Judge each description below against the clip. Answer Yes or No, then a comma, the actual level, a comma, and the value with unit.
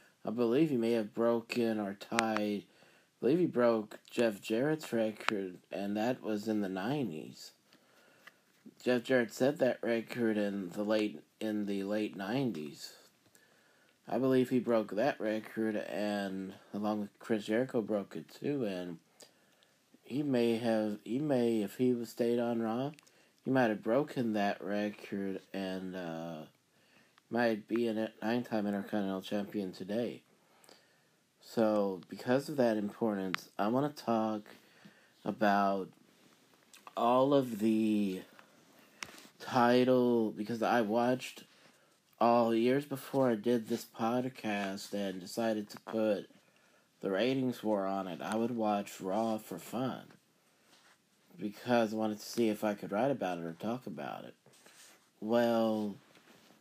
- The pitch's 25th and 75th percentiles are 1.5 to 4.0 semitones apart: Yes, average, 2.8 semitones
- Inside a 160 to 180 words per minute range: No, average, 140 wpm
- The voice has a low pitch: Yes, low, 110 Hz